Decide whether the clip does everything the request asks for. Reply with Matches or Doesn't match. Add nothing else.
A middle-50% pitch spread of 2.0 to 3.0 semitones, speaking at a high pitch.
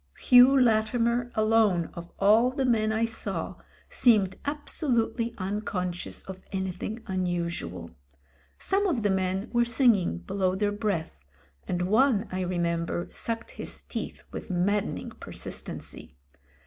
Doesn't match